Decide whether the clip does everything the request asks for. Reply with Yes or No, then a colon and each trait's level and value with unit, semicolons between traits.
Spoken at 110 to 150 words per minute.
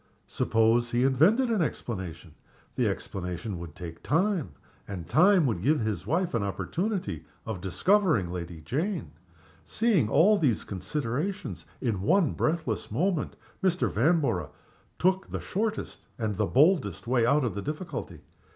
Yes: average, 140 wpm